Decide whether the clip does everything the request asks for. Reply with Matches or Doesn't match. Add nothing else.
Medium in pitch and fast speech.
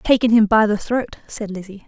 Doesn't match